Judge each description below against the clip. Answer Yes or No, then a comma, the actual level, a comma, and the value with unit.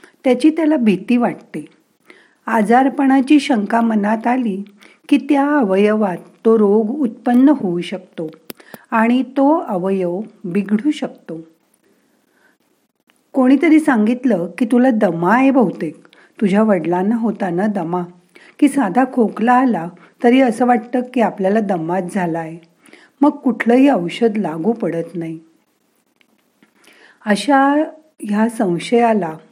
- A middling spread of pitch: No, wide, 5.8 semitones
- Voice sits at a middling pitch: No, high, 225 Hz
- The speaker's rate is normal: Yes, average, 110 wpm